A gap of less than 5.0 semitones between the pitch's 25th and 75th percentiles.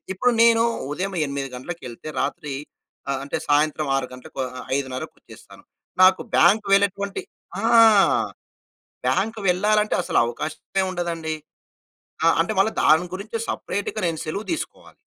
No: wide, 5.5 semitones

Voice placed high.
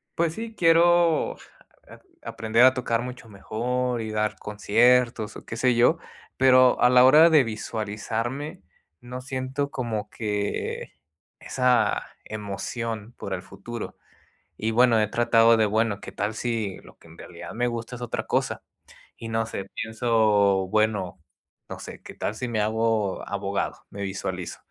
No: low, 115 Hz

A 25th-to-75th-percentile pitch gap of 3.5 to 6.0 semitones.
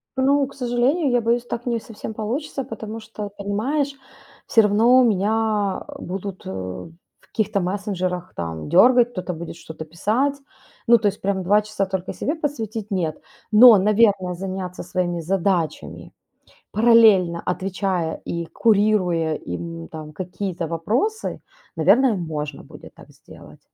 Yes: average, 4.7 semitones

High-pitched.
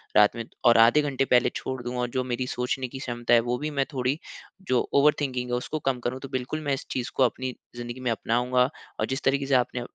No: low, 125 Hz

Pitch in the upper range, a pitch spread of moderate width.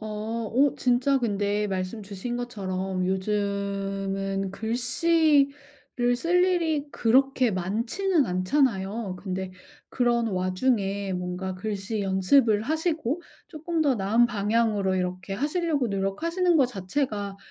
No: high, 220 Hz; wide, 5.7 semitones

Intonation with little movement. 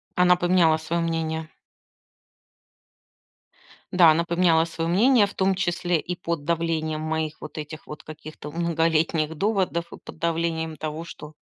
Yes: narrow, 1.7 semitones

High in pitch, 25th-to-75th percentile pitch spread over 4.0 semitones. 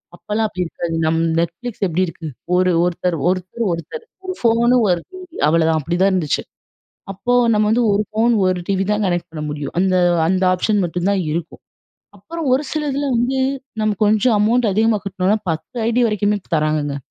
Yes: high, 195 Hz; average, 4.7 semitones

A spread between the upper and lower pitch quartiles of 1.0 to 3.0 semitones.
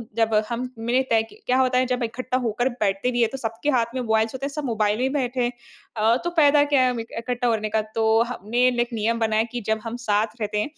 Yes: narrow, 2.4 semitones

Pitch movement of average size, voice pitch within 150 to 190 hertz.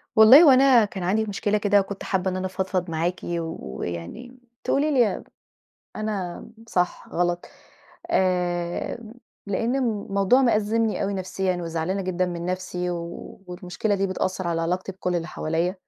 Yes: average, 3.2 semitones; medium, 185 Hz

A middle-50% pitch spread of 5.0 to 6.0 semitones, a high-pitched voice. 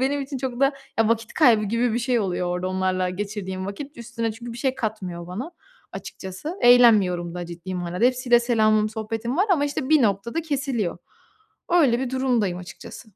Yes: wide, 5.5 semitones; high, 230 Hz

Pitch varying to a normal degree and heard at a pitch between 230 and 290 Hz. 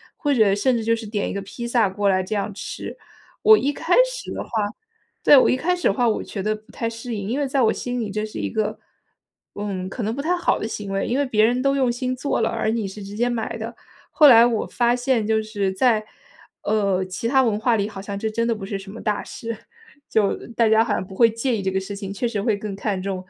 No: average, 3.2 semitones; high, 220 Hz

